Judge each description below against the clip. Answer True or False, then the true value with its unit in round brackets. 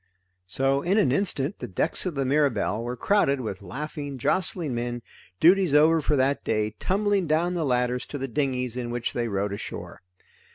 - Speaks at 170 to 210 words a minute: True (180 wpm)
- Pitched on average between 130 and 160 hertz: True (135 Hz)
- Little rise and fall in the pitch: False (5.0 semitones)